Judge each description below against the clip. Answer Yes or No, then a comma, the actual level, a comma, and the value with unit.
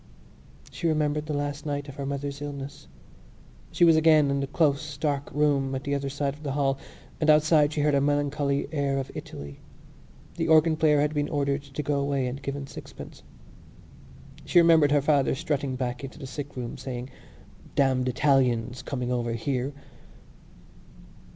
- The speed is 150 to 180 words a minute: Yes, average, 170 wpm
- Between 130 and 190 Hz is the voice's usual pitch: Yes, medium, 140 Hz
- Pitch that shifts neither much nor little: No, narrow, 1.7 semitones